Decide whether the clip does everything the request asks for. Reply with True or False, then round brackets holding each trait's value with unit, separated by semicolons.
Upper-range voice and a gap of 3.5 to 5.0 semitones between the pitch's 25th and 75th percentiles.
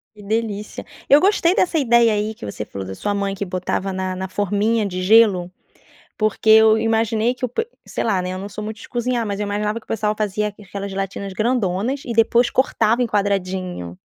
False (210 Hz; 2.8 semitones)